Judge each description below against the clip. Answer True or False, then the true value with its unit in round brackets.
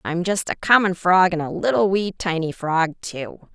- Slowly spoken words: False (205 wpm)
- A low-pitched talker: False (175 Hz)